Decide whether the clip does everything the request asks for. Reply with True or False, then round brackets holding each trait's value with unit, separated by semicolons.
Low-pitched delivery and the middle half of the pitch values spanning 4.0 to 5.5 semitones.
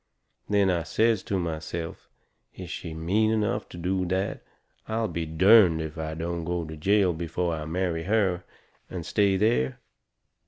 False (90 Hz; 3.3 semitones)